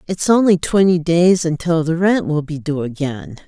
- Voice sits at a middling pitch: Yes, medium, 165 Hz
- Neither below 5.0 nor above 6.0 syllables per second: No, 4.7 syllables/s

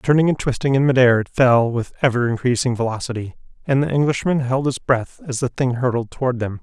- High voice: No, low, 125 Hz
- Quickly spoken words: Yes, fast, 210 wpm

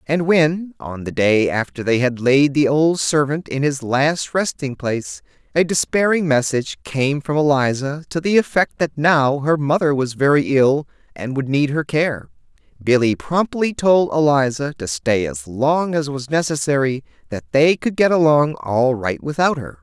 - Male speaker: Yes, male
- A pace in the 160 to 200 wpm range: Yes, average, 170 wpm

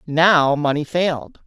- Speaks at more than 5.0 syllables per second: No, 3.8 syllables/s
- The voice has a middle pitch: Yes, medium, 155 Hz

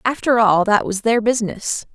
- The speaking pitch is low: No, high, 225 Hz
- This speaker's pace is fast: No, average, 185 wpm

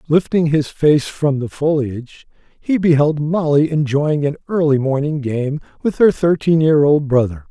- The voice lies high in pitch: No, medium, 150 Hz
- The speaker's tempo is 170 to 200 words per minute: No, average, 160 wpm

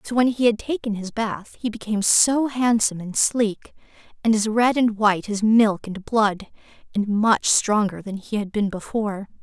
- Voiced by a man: No, female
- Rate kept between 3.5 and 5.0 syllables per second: Yes, 4.7 syllables/s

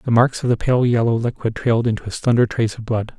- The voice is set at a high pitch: No, low, 115 Hz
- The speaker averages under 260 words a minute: No, fast, 265 wpm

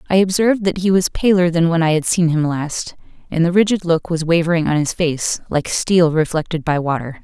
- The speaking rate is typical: No, fast, 225 wpm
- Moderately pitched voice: Yes, medium, 170 Hz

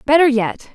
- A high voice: Yes, very high, 270 Hz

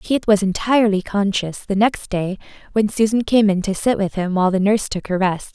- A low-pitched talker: No, high, 200 Hz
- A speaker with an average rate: No, fast, 225 wpm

